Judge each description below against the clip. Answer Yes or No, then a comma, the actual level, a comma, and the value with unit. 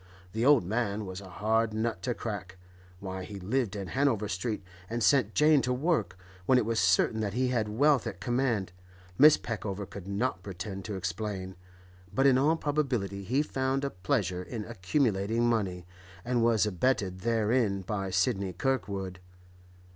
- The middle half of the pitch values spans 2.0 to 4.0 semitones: No, average, 4.7 semitones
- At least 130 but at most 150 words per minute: No, average, 165 wpm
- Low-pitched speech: Yes, low, 110 Hz